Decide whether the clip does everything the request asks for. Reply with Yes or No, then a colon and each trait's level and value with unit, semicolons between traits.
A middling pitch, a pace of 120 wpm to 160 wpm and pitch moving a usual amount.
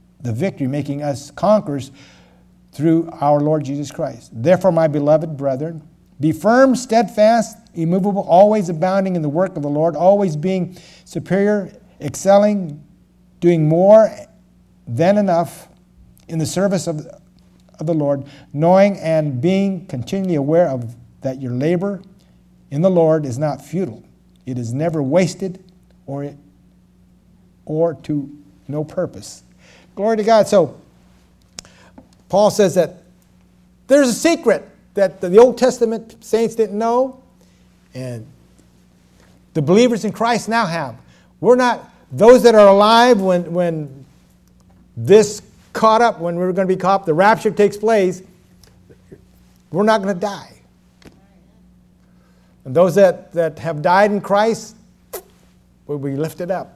No: medium, 170 Hz; slow, 135 wpm; wide, 6.2 semitones